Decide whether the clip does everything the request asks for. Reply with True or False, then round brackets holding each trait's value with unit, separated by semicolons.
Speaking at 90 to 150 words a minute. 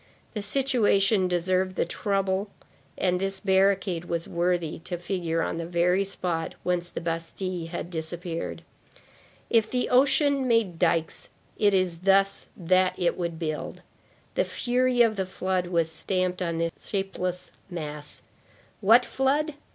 True (140 wpm)